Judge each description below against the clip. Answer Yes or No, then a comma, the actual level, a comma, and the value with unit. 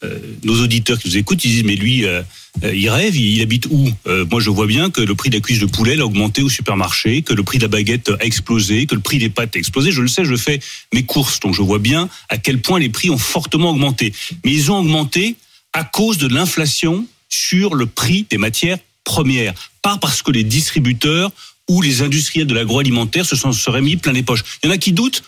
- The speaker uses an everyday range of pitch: No, wide, 6.0 semitones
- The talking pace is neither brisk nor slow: No, fast, 250 wpm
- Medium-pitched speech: No, low, 125 Hz